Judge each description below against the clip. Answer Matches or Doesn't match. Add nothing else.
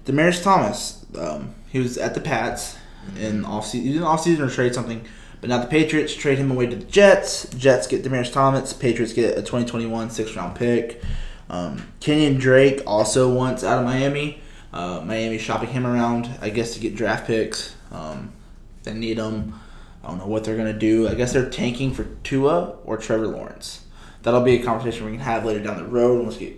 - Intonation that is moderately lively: Matches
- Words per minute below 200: Doesn't match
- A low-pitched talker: Matches